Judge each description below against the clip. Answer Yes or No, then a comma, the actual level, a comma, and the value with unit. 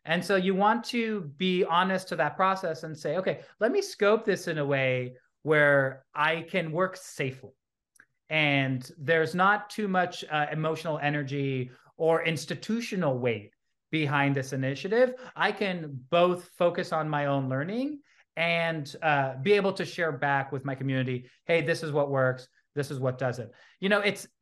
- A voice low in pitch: No, medium, 160 Hz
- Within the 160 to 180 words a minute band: Yes, average, 170 wpm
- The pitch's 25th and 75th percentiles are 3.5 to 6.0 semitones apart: Yes, average, 5.3 semitones